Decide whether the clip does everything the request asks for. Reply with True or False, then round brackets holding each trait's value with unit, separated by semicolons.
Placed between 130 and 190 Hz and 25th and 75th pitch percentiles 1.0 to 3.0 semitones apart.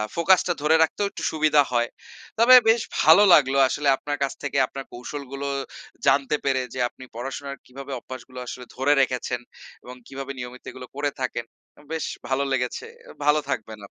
True (140 Hz; 2.6 semitones)